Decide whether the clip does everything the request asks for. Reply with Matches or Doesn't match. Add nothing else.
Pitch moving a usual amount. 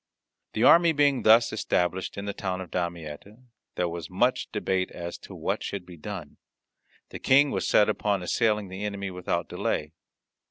Matches